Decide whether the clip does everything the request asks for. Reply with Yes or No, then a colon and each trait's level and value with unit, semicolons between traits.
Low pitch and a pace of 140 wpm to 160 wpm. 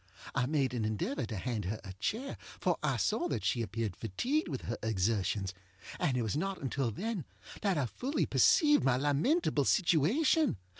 No: low, 130 Hz; average, 170 wpm